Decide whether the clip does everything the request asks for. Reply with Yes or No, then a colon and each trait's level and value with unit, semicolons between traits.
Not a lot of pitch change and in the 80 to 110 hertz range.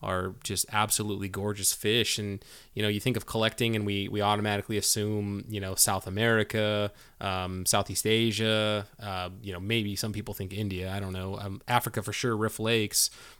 Yes: narrow, 1.9 semitones; low, 105 Hz